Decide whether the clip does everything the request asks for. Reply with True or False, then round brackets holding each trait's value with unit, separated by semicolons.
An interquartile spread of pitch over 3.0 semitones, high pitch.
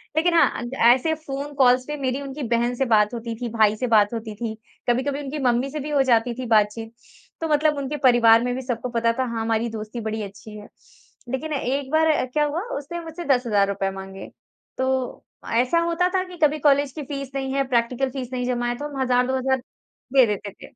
True (3.4 semitones; 255 Hz)